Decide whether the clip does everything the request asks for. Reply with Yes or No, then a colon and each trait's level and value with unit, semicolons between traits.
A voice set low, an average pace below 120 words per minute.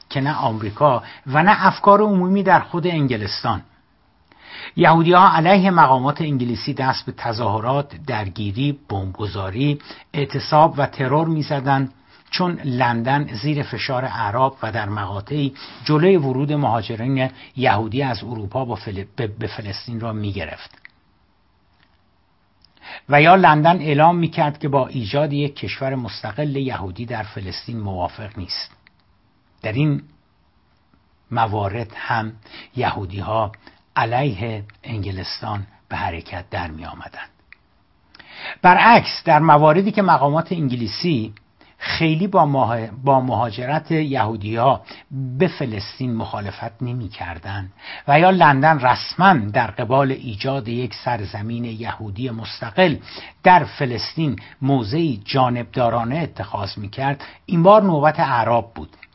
Yes: low, 125 Hz; average, 110 wpm